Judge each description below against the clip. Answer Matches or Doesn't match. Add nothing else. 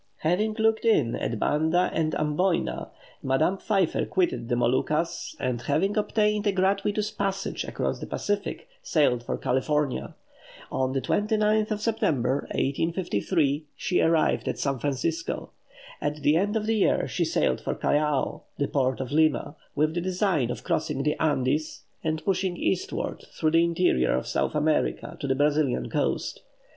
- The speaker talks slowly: Doesn't match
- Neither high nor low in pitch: Matches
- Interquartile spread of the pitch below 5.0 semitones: Doesn't match